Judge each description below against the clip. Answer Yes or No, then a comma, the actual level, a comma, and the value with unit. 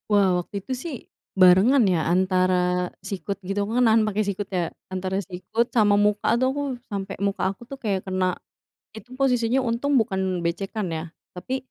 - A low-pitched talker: No, high, 200 Hz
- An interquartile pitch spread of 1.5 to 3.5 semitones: No, average, 4.0 semitones